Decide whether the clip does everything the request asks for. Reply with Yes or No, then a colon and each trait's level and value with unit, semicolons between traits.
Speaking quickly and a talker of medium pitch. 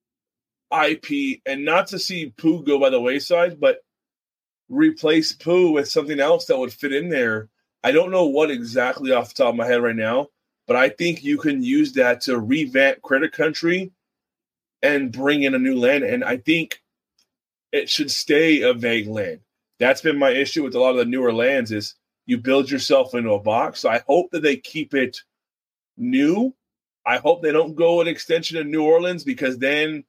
No: average, 195 wpm; medium, 160 Hz